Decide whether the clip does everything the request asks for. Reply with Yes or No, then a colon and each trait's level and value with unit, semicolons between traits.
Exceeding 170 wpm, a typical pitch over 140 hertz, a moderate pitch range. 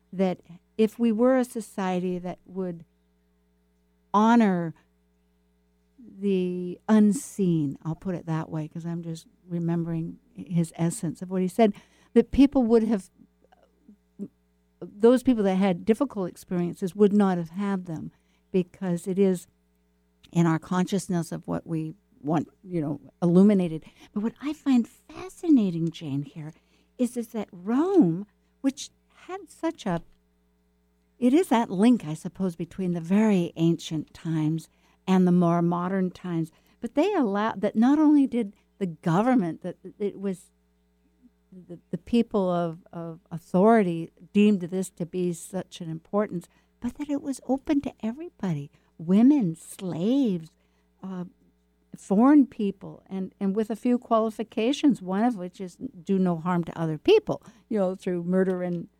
No: average, 145 wpm; medium, 185 Hz; average, 5.0 semitones